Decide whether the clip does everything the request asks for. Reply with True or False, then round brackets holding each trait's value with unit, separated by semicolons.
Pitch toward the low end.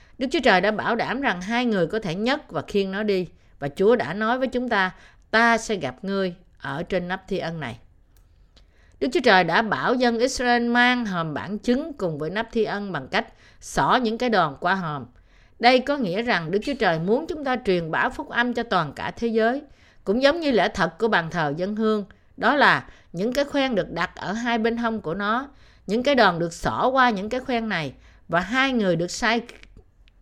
False (215 Hz)